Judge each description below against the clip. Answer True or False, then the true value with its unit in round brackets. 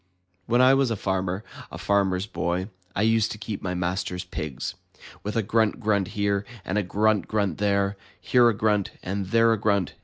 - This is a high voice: False (100 Hz)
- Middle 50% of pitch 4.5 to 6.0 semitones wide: False (2.7 semitones)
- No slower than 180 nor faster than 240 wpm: True (190 wpm)